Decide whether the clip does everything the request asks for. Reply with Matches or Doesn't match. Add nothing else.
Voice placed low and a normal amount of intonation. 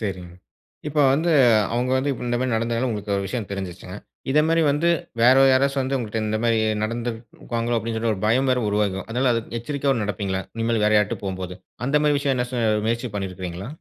Matches